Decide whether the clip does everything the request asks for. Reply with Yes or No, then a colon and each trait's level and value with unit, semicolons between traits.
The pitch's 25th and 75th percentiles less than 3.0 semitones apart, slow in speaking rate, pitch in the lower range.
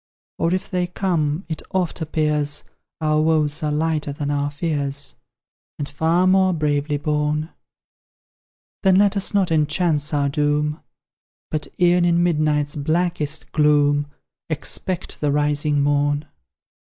No: narrow, 2.6 semitones; slow, 130 wpm; medium, 150 Hz